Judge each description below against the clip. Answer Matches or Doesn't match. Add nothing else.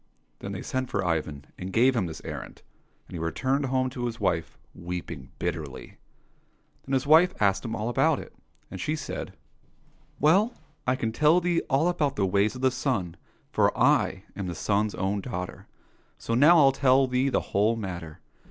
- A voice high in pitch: Doesn't match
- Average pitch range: Doesn't match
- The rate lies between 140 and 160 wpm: Doesn't match